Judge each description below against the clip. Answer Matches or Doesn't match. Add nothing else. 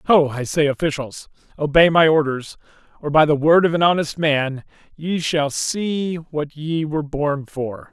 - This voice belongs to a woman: Doesn't match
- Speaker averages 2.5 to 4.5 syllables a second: Matches